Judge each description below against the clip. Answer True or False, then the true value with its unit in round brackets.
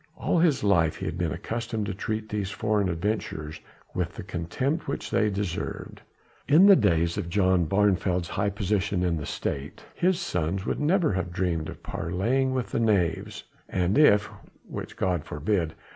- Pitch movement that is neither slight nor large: True (4.0 semitones)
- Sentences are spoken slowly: False (175 wpm)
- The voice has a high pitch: False (100 Hz)